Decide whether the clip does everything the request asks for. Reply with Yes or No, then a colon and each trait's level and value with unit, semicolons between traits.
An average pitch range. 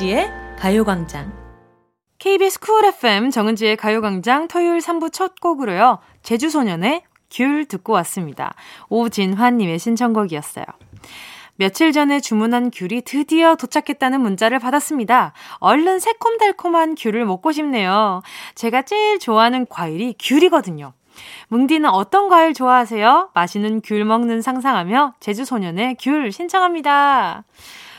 No: wide, 6.6 semitones